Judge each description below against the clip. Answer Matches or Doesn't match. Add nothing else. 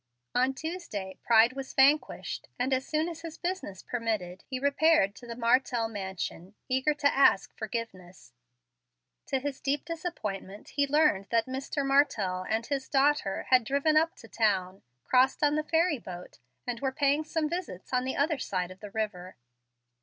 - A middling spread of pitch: Doesn't match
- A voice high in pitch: Matches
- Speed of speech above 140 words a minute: Matches